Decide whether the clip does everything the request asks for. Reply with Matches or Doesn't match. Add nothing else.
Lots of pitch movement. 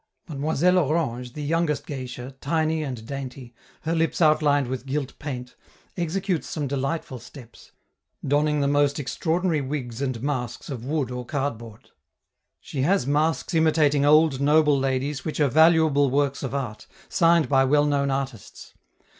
Doesn't match